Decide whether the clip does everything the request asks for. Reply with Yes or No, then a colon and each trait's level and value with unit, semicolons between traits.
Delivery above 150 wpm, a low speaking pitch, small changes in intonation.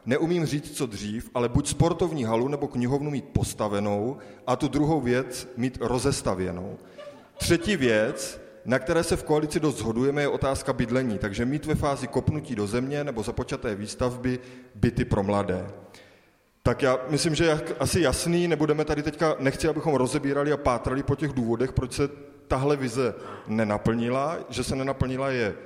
No: average, 160 wpm; low, 130 Hz; average, 3.3 semitones